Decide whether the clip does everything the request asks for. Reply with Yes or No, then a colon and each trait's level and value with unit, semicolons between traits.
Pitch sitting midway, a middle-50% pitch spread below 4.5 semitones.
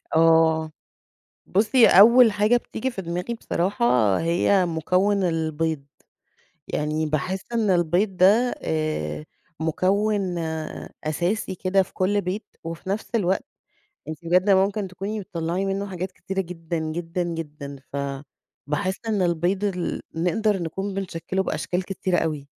Yes: medium, 180 Hz; average, 3.4 semitones